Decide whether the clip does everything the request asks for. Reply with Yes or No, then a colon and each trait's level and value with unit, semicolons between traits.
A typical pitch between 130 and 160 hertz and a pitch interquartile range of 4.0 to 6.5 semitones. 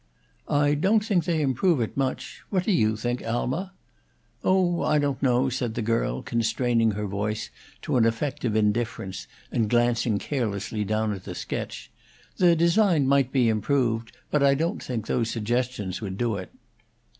No: low, 120 Hz; average, 4.7 semitones